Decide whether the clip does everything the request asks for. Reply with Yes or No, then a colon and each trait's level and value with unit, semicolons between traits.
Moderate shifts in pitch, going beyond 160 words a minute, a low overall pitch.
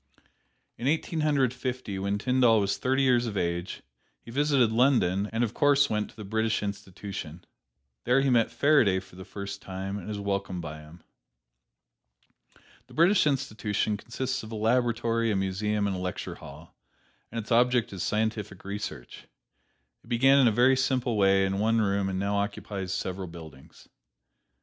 Yes: average, 4.2 semitones; average, 170 wpm; low, 105 Hz